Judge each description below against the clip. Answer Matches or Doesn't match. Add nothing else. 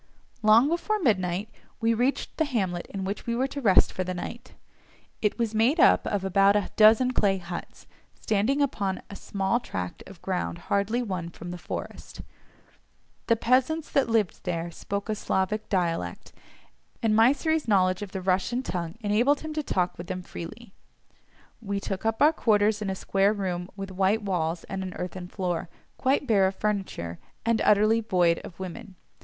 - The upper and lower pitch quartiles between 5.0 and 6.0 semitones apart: Doesn't match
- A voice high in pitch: Matches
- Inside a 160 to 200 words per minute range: Matches